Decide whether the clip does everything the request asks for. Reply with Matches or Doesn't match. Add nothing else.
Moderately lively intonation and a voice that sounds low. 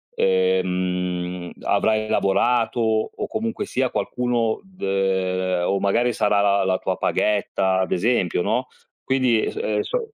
Matches